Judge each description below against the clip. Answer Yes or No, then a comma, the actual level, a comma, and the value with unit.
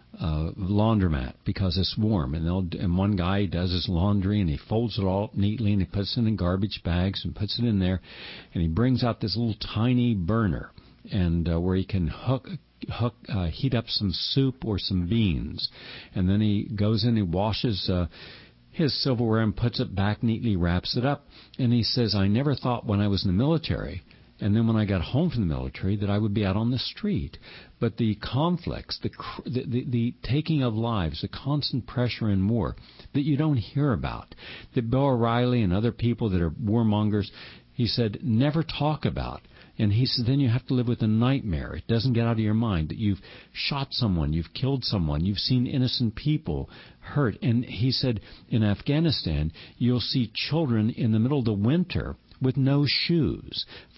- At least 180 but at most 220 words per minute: Yes, average, 200 wpm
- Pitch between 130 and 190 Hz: No, low, 110 Hz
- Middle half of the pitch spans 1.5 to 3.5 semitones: No, average, 4.5 semitones